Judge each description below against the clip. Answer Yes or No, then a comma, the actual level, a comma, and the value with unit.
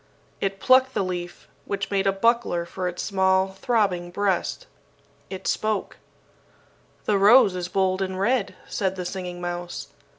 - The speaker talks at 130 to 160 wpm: Yes, average, 145 wpm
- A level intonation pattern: Yes, narrow, 1.9 semitones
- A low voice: No, high, 190 Hz